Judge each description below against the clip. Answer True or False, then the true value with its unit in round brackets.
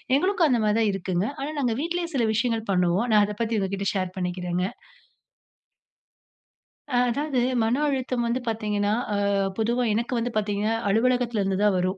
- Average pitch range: True (3.9 semitones)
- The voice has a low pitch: False (220 Hz)